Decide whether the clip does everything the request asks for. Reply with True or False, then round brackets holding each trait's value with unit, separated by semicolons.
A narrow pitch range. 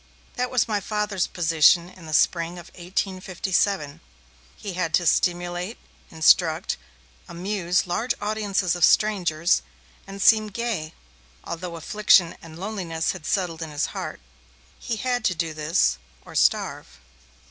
False (3.7 semitones)